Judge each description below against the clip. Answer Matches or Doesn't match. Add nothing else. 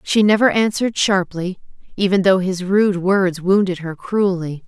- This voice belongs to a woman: Matches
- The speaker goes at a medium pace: Matches